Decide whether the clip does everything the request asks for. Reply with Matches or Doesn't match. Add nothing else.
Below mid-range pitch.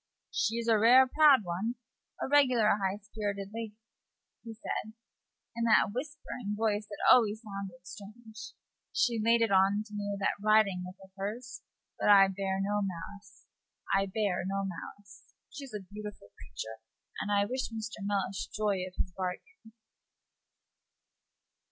Doesn't match